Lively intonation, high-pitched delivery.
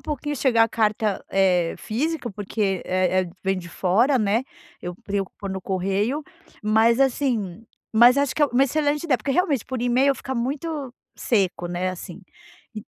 Yes: wide, 5.8 semitones; high, 225 Hz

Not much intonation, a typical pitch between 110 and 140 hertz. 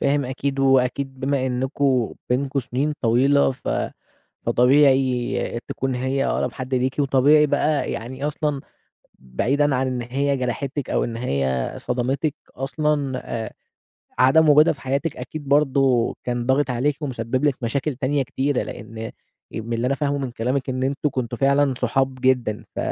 Yes: narrow, 2.1 semitones; low, 135 Hz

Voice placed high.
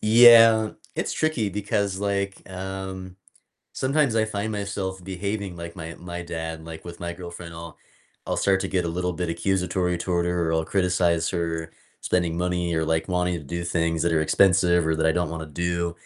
No: very low, 90 Hz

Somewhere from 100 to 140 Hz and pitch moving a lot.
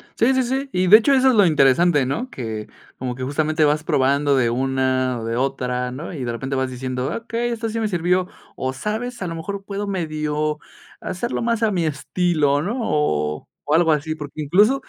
No: medium, 155 Hz; wide, 7.6 semitones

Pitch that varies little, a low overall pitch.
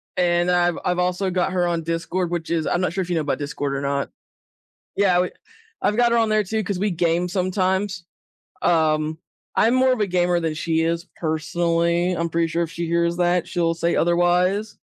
No: narrow, 1.7 semitones; medium, 175 Hz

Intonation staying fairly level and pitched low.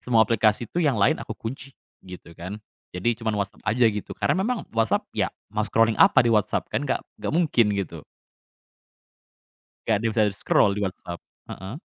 No: average, 3.0 semitones; low, 110 Hz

